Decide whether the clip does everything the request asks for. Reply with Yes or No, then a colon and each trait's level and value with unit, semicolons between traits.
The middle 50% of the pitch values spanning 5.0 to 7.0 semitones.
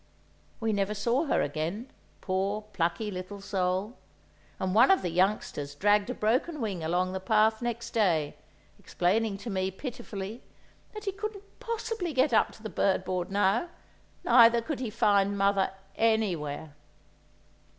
No: average, 3.9 semitones